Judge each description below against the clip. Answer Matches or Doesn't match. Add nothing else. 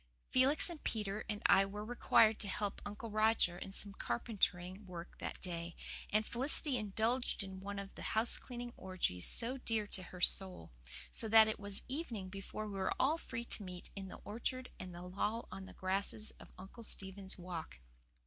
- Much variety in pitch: Doesn't match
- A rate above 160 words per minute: Matches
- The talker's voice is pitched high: Matches